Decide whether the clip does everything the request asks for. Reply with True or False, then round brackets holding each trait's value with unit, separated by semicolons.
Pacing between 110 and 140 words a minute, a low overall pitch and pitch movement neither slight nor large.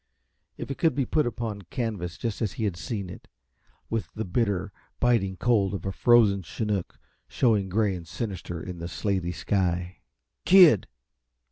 False (160 wpm; 100 Hz; 4.1 semitones)